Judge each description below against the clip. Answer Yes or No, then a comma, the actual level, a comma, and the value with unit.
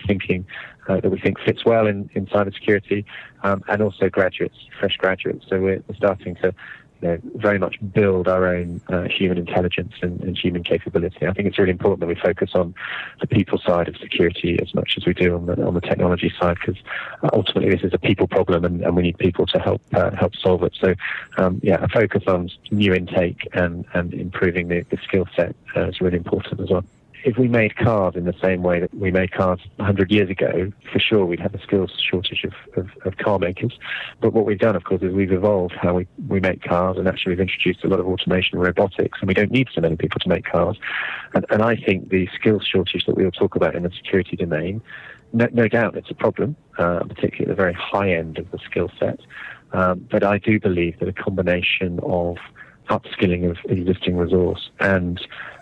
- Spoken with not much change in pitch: Yes, narrow, 2.0 semitones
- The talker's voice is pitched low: Yes, very low, 95 Hz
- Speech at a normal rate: No, fast, 225 wpm